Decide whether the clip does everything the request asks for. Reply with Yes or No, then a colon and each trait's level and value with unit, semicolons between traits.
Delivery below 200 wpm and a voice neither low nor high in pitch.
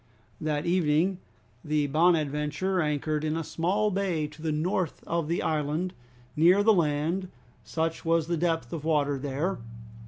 Yes: average, 150 wpm; medium, 160 Hz